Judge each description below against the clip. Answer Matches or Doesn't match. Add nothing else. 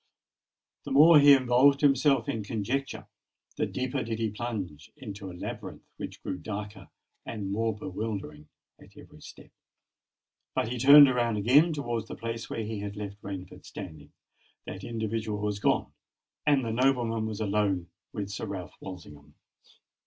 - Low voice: Matches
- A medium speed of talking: Matches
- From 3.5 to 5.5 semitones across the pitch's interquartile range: Matches